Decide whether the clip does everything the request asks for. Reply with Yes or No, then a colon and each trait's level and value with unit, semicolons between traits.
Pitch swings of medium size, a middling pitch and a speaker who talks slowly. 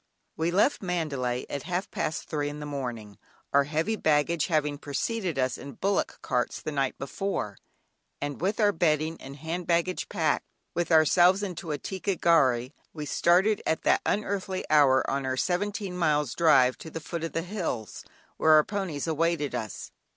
No: average, 4.1 semitones; medium, 160 Hz; average, 180 wpm